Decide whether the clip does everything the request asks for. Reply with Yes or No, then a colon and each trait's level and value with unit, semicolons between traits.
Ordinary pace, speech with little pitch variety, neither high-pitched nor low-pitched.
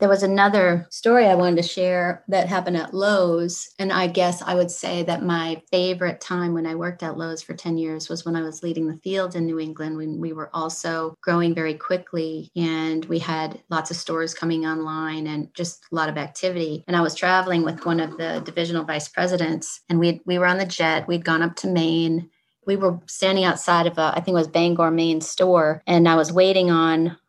No: fast, 225 wpm; narrow, 1.8 semitones; medium, 170 Hz